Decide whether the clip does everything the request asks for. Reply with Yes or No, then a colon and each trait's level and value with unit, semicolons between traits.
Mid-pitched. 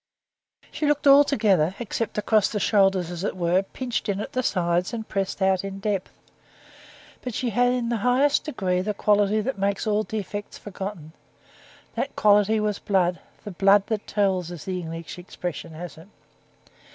No: high, 200 Hz